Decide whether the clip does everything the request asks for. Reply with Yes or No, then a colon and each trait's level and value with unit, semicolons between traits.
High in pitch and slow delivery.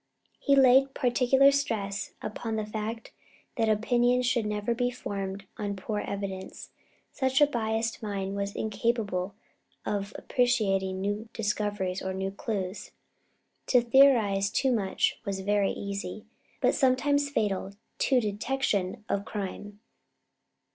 Yes: high, 210 Hz; slow, 125 wpm